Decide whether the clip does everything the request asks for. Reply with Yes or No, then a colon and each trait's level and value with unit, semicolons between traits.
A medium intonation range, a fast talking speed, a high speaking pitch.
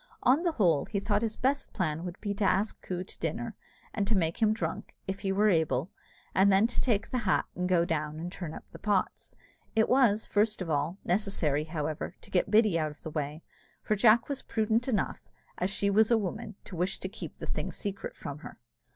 Yes: average, 4.4 semitones; fast, 225 wpm; high, 195 Hz